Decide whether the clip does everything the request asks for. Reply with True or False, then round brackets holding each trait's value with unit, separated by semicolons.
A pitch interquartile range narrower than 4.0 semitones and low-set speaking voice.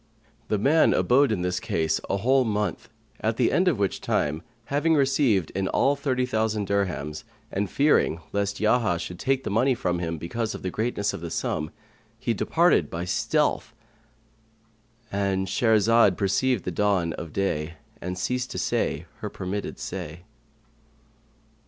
False (5.1 semitones; 105 Hz)